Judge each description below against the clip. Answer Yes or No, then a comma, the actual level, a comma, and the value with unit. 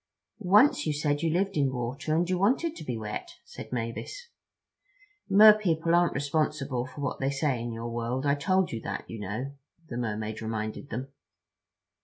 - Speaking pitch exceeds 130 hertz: Yes, medium, 140 Hz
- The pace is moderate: Yes, average, 180 wpm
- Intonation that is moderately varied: No, wide, 6.6 semitones